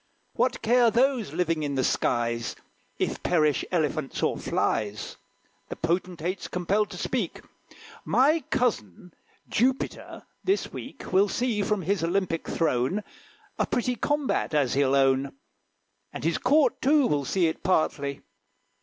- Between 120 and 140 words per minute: Yes, slow, 135 wpm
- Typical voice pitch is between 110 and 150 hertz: No, medium, 175 Hz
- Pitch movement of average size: No, wide, 8.5 semitones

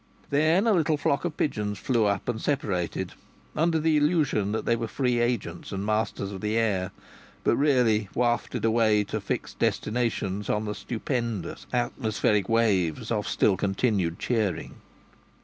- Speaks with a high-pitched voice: No, low, 110 Hz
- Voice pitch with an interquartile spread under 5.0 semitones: Yes, average, 3.7 semitones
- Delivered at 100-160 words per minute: Yes, average, 150 wpm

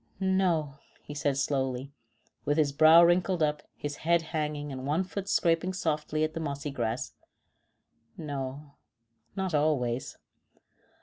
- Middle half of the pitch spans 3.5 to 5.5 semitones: No, average, 2.8 semitones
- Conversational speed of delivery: No, slow, 130 wpm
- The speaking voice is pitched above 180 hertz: No, medium, 150 Hz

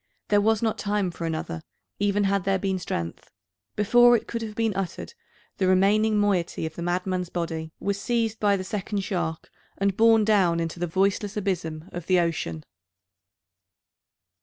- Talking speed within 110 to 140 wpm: No, average, 165 wpm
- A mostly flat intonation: No, average, 3.3 semitones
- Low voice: No, high, 195 Hz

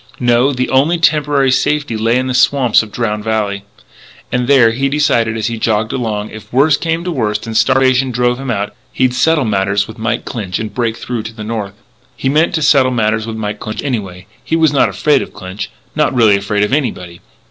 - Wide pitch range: No, average, 3.9 semitones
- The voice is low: Yes, low, 120 Hz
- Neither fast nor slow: No, fast, 215 wpm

